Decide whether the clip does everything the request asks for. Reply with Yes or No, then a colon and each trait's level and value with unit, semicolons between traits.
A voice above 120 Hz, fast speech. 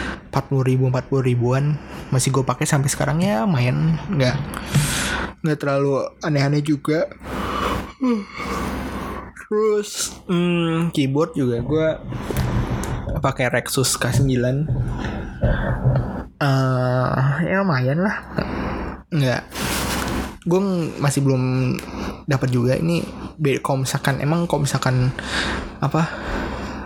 No: low, 135 Hz; average, 95 wpm